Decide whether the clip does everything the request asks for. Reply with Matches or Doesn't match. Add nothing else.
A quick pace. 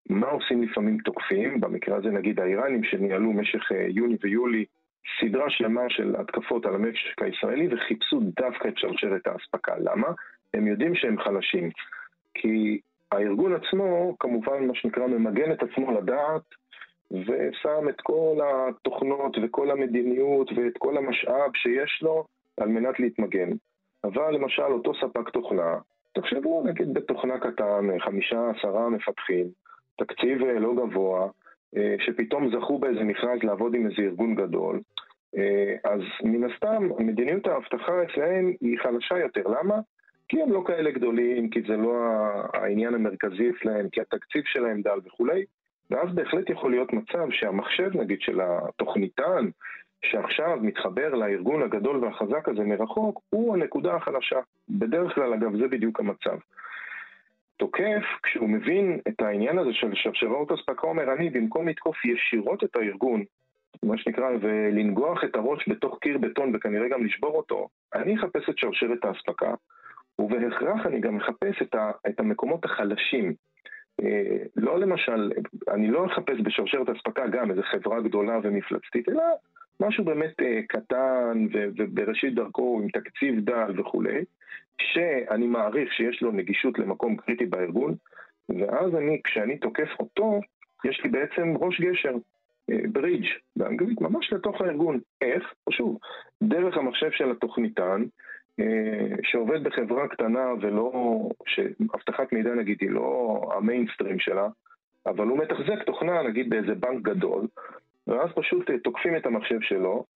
Doesn't match